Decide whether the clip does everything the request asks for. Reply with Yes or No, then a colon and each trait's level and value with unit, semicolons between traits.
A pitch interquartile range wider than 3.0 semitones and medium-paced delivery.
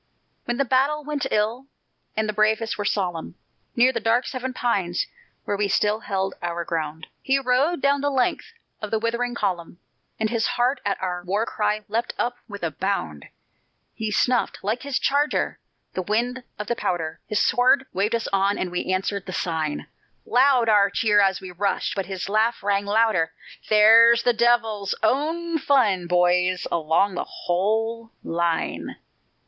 Yes: average, 4.4 semitones; average, 170 wpm